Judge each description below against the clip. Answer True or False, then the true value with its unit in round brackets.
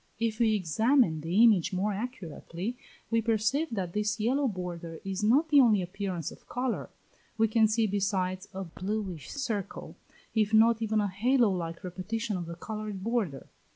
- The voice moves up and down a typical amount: True (3.7 semitones)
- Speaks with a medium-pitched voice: False (210 Hz)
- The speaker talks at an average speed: True (165 wpm)